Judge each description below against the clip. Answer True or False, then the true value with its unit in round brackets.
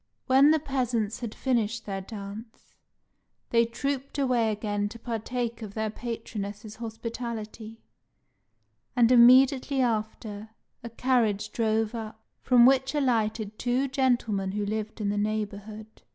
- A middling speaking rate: False (125 wpm)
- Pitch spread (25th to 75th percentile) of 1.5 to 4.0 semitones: True (2.7 semitones)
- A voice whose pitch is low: False (225 Hz)